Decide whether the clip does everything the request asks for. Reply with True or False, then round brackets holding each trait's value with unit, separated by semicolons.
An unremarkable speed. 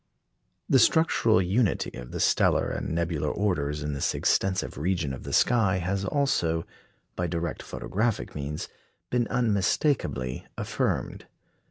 False (130 wpm)